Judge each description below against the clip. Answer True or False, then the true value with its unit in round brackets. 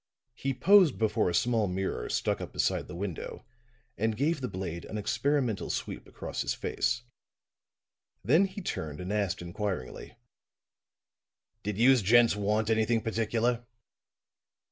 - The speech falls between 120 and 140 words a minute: True (135 wpm)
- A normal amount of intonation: True (3.8 semitones)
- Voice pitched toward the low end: True (110 Hz)